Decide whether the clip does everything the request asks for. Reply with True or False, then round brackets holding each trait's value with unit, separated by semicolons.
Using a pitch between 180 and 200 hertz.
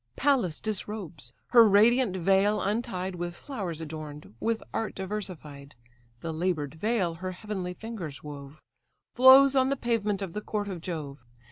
True (190 Hz)